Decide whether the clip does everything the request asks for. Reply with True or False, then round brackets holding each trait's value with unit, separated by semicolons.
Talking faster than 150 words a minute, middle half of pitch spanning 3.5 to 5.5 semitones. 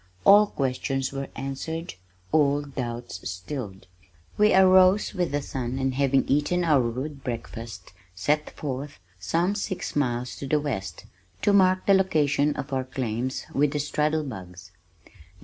False (145 wpm; 3.8 semitones)